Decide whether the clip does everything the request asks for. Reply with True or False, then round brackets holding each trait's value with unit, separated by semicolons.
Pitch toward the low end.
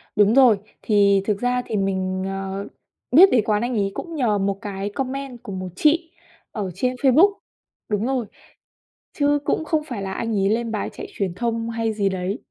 False (220 Hz)